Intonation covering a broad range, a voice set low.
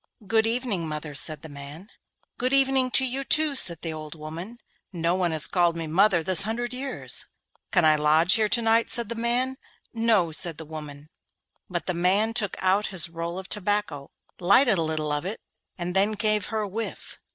No: wide, 5.7 semitones; high, 190 Hz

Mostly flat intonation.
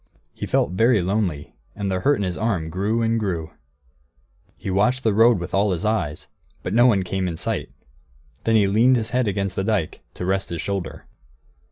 No: average, 3.5 semitones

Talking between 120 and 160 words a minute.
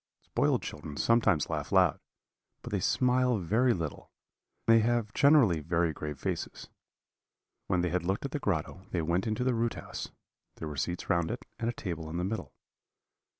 No: average, 180 wpm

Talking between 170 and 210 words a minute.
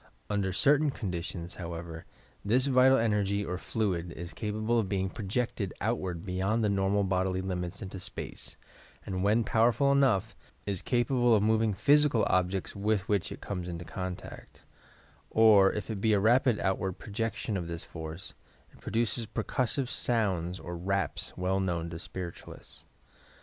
No: average, 155 wpm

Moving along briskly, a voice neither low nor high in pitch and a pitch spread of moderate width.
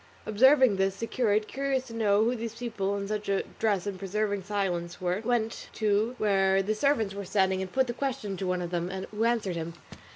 No: fast, 220 wpm; high, 205 Hz; average, 3.0 semitones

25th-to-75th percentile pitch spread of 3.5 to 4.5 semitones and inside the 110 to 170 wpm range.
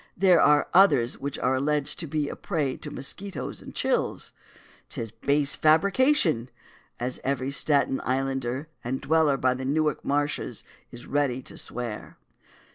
No: average, 3.1 semitones; average, 150 wpm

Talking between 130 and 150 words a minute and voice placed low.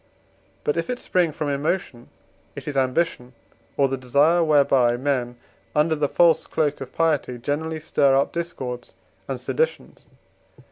No: average, 145 wpm; medium, 145 Hz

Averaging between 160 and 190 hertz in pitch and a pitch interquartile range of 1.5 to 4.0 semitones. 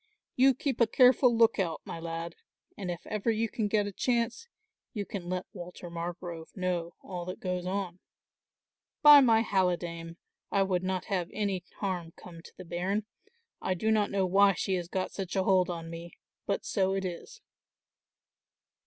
Yes: medium, 185 Hz; average, 3.1 semitones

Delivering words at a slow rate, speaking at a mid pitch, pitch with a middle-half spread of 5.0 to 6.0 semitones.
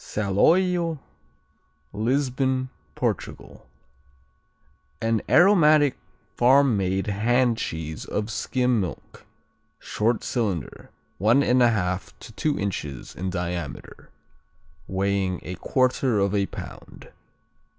No: slow, 90 wpm; low, 110 Hz; average, 5.3 semitones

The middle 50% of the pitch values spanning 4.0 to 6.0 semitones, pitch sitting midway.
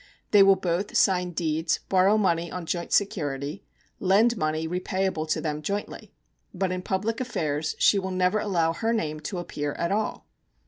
No: average, 3.6 semitones; medium, 180 Hz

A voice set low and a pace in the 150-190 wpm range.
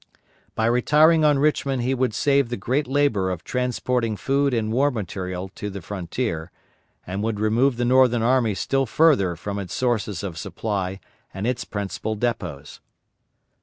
Yes: low, 115 Hz; average, 160 wpm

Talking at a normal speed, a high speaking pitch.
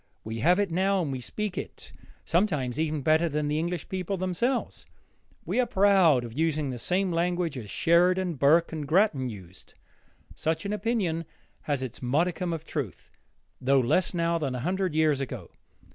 No: average, 175 wpm; medium, 165 Hz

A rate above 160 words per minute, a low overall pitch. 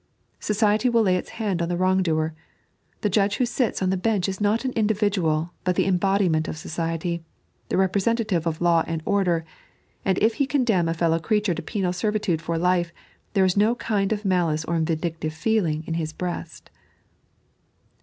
No: average, 185 wpm; medium, 185 Hz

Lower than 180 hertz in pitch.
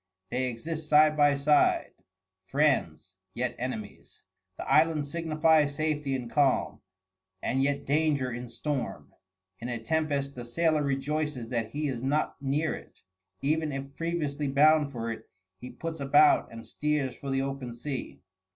Yes: medium, 140 Hz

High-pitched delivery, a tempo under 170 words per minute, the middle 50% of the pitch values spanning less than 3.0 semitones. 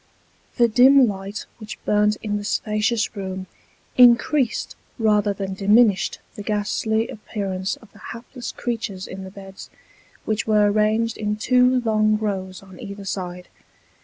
Yes: high, 210 Hz; average, 140 wpm; narrow, 2.4 semitones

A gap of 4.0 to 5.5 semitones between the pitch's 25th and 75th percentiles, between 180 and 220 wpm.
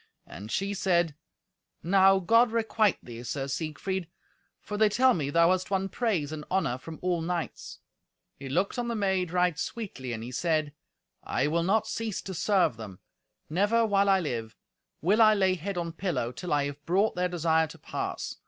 Yes: average, 4.7 semitones; average, 185 wpm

